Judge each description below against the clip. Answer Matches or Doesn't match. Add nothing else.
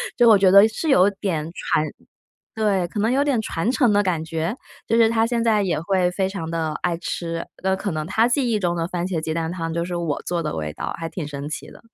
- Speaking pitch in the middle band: Matches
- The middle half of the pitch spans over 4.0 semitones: Matches